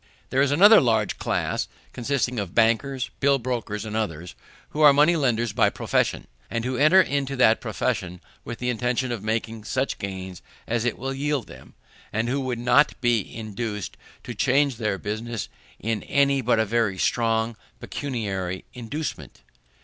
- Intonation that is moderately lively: Yes, average, 3.7 semitones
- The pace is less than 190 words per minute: Yes, average, 165 wpm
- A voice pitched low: Yes, low, 120 Hz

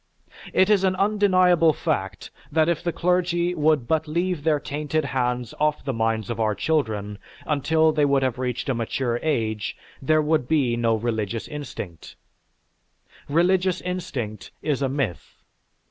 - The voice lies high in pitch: No, medium, 145 Hz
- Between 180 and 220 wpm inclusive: No, average, 150 wpm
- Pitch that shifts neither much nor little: No, wide, 5.7 semitones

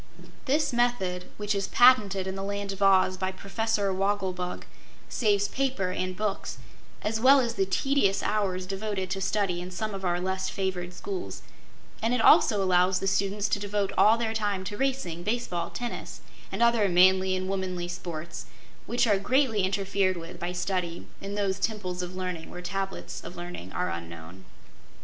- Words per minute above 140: Yes, average, 175 wpm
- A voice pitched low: No, high, 195 Hz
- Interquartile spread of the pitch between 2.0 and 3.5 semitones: Yes, narrow, 2.4 semitones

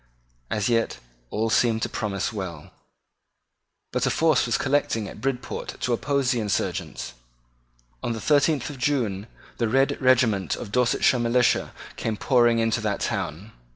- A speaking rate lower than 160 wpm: Yes, average, 150 wpm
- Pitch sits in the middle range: No, low, 115 Hz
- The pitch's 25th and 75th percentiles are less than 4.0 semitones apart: Yes, average, 3.4 semitones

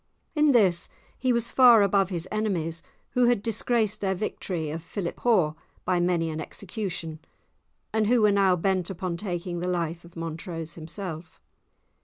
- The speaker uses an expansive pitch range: No, average, 4.1 semitones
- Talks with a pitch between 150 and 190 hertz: Yes, medium, 185 Hz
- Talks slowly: No, average, 155 wpm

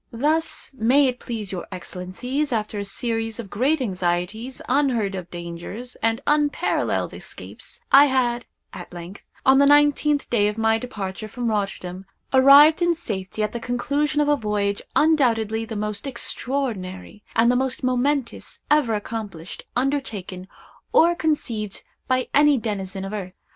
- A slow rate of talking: No, average, 150 wpm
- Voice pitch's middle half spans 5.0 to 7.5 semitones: Yes, average, 5.3 semitones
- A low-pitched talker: No, high, 230 Hz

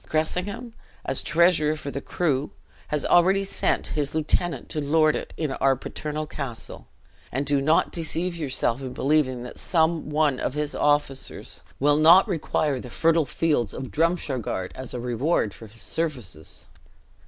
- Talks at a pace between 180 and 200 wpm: No, average, 155 wpm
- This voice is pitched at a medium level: Yes, medium, 150 Hz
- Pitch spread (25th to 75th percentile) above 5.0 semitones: No, average, 3.6 semitones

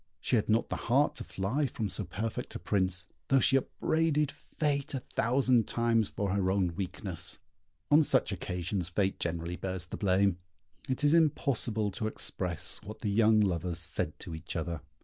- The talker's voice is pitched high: No, low, 100 Hz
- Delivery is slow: No, average, 175 wpm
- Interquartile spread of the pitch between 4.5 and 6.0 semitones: Yes, wide, 5.5 semitones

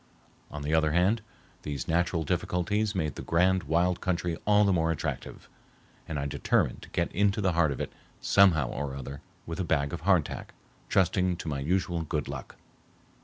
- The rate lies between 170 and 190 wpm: Yes, average, 180 wpm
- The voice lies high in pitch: No, very low, 85 Hz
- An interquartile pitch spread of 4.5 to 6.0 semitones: No, average, 3.3 semitones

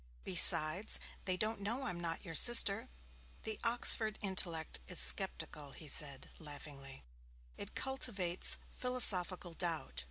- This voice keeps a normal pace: No, slow, 120 wpm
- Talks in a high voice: No, medium, 180 Hz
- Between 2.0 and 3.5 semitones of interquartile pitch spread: No, average, 5.3 semitones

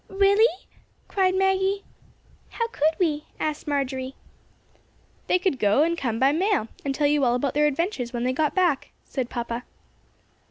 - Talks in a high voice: Yes, very high, 295 Hz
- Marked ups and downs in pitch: Yes, wide, 6.3 semitones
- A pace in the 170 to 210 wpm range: No, average, 160 wpm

